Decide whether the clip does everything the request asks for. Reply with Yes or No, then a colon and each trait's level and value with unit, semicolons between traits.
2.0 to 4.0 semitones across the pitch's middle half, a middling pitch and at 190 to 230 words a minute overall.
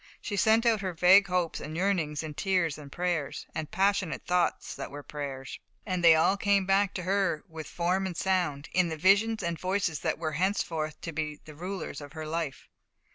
Yes: average, 3.7 semitones; medium, 175 Hz; average, 200 wpm